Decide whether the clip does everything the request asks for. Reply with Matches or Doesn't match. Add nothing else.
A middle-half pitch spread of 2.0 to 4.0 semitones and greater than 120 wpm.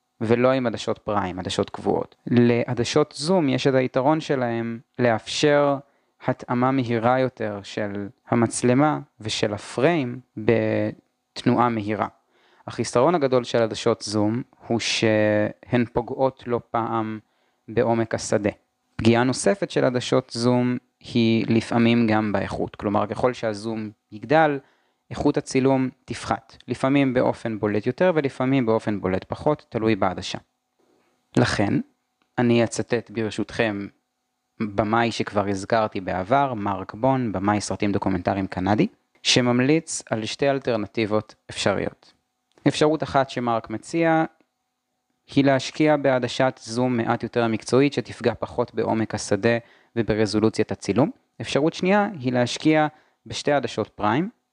Doesn't match